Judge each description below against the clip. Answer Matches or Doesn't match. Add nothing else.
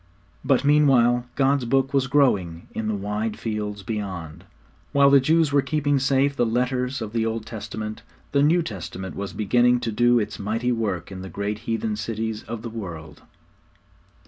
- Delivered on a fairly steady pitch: Doesn't match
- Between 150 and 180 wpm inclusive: Matches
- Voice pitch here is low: Matches